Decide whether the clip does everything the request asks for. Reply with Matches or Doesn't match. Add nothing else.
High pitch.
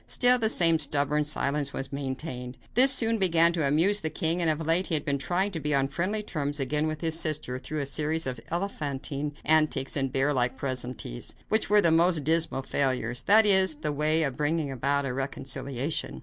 Doesn't match